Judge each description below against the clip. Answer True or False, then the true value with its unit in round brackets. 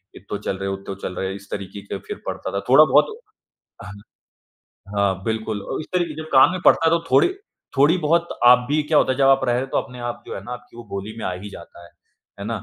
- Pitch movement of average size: False (6.4 semitones)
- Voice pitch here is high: False (120 Hz)